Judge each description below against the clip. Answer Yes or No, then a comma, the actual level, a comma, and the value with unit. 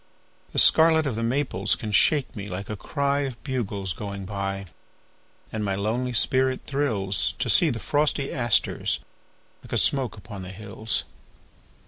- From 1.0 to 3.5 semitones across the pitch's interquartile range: No, wide, 5.5 semitones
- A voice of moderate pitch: No, low, 110 Hz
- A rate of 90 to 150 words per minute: Yes, average, 140 wpm